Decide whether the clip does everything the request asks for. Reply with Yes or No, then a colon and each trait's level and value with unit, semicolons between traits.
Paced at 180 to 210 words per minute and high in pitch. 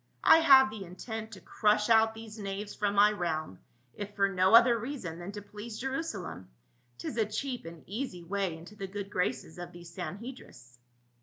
Yes: average, 185 wpm; high, 205 Hz